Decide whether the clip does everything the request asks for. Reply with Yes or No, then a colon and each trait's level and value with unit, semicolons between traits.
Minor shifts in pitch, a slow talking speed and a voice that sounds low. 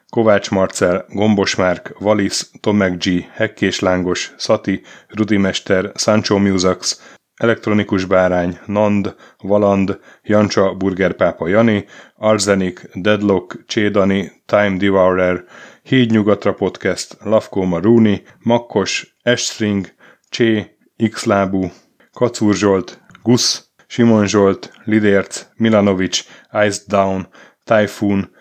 Yes: narrow, 2.0 semitones; slow, 90 wpm; low, 100 Hz